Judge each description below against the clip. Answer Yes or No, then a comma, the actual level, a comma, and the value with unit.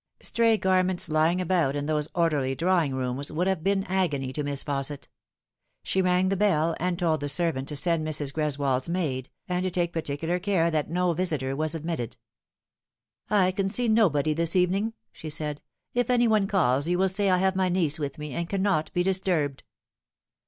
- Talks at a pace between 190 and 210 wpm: Yes, average, 195 wpm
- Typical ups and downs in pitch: Yes, average, 4.2 semitones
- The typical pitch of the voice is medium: Yes, medium, 170 Hz